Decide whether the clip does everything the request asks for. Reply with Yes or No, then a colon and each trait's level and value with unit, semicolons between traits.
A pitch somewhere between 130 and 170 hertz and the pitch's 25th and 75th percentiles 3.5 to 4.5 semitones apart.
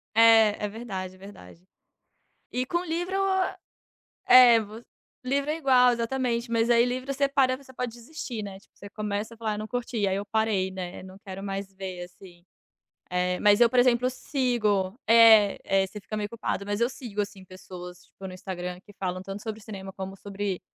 No: high, 210 Hz; average, 4.0 semitones